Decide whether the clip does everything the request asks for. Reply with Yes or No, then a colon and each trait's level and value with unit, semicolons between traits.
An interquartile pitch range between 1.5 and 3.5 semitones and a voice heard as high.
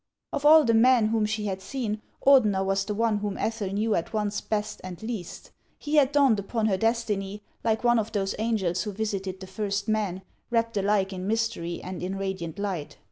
Yes: average, 2.8 semitones; high, 210 Hz